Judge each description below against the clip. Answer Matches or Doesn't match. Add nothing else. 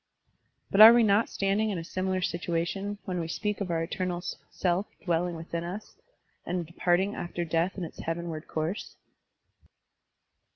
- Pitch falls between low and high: Matches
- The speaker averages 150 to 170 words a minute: Matches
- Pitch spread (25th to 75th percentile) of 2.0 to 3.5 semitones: Matches